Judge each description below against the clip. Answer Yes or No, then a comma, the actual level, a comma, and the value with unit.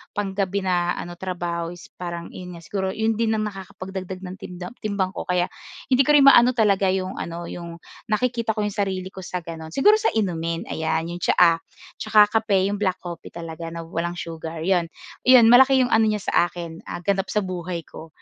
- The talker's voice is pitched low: No, medium, 185 Hz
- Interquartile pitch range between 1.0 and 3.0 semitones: No, average, 3.4 semitones